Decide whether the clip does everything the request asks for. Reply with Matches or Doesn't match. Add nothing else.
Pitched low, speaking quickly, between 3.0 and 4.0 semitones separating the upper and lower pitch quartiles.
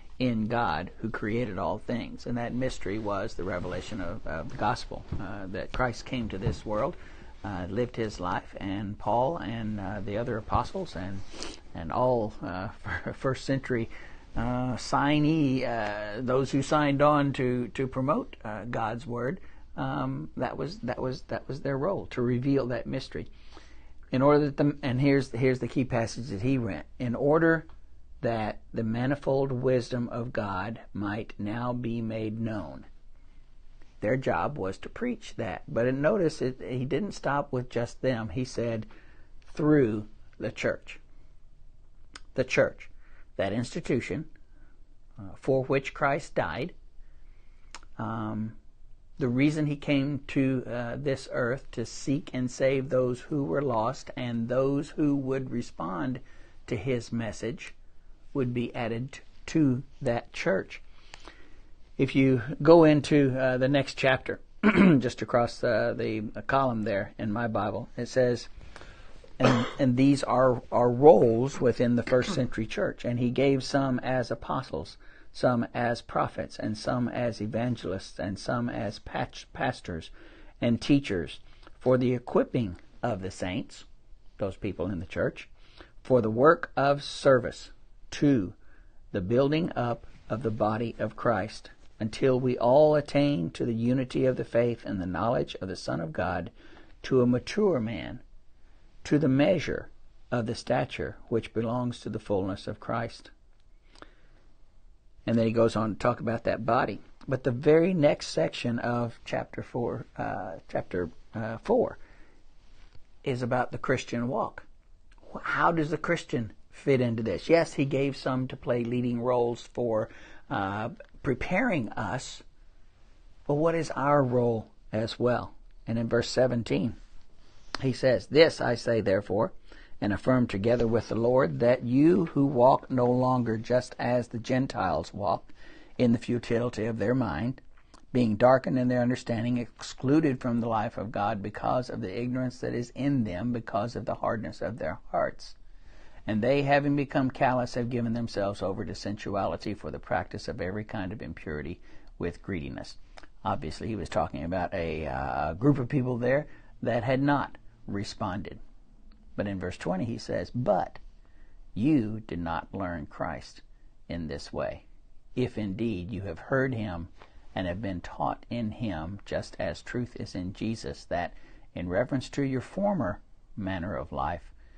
Doesn't match